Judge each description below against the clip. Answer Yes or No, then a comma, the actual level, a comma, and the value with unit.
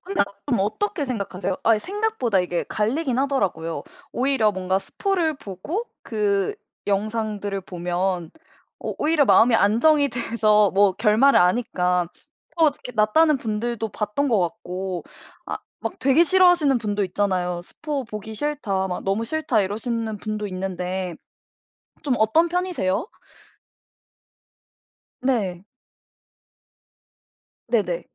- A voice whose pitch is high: Yes, high, 215 Hz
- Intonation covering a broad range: Yes, wide, 6.3 semitones